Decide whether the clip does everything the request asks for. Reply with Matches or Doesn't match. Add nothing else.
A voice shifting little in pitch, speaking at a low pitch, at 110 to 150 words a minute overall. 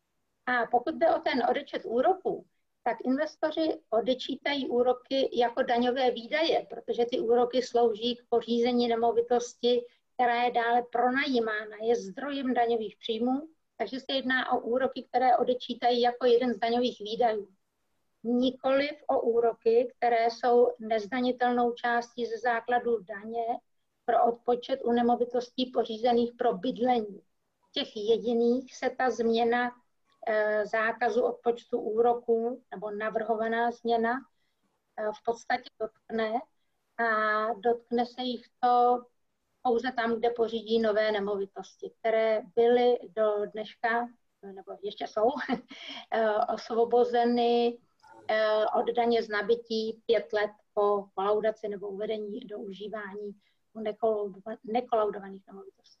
Doesn't match